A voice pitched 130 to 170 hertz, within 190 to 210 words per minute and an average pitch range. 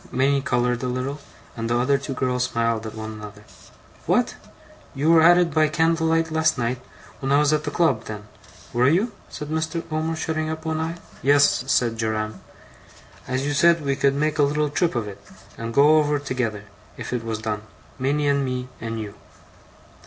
Yes: medium, 140 Hz; average, 195 wpm; average, 5.0 semitones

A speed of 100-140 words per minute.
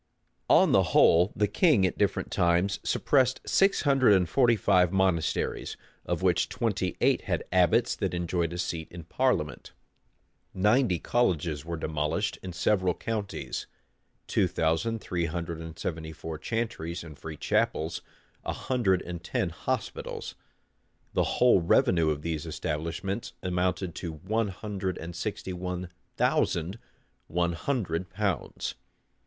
Yes: slow, 135 wpm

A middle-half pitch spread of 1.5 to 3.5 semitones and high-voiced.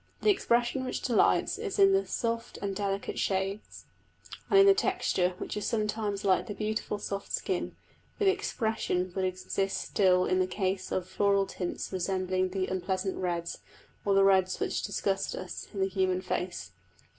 Yes: average, 2.7 semitones; high, 195 Hz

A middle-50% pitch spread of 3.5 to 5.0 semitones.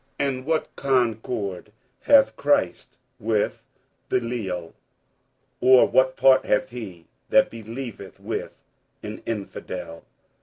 Yes: average, 4.7 semitones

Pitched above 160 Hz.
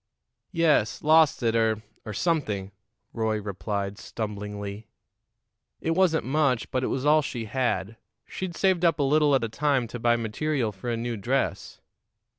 No: low, 120 Hz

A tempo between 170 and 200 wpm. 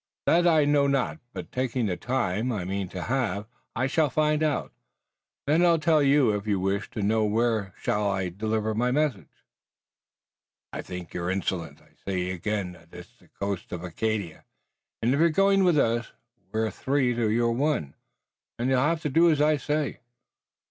Yes: average, 180 wpm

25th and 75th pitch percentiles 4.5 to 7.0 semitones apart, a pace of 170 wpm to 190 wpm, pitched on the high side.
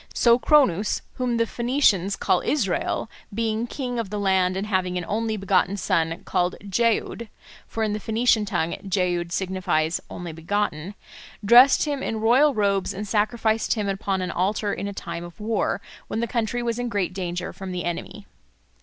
No: average, 3.9 semitones; average, 175 wpm; high, 205 Hz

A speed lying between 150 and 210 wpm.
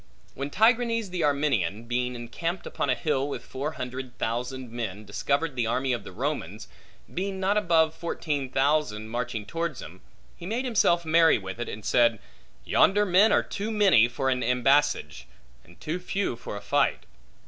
Yes: average, 170 wpm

